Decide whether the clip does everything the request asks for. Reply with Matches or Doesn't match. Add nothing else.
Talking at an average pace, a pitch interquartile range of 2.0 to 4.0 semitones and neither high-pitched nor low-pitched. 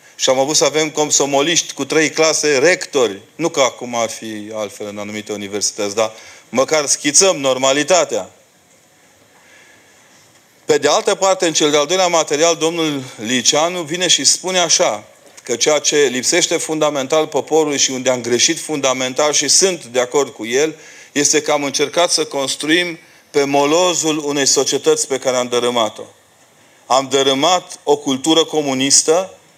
Matches